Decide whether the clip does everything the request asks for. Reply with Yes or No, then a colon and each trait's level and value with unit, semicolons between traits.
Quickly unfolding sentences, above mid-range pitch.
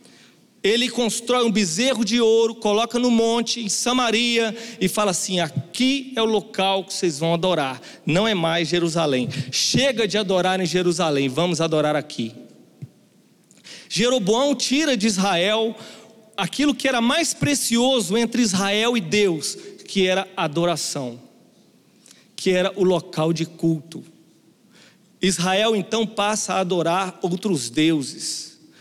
No: average, 135 wpm; high, 195 Hz